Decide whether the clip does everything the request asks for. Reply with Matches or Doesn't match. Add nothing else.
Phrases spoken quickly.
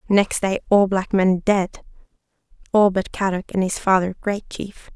Doesn't match